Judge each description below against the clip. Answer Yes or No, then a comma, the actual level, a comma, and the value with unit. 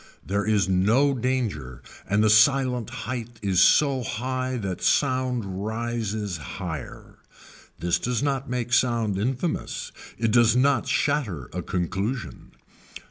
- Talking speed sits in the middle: No, slow, 125 wpm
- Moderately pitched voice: No, low, 115 Hz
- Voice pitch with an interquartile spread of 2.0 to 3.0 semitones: No, average, 4.5 semitones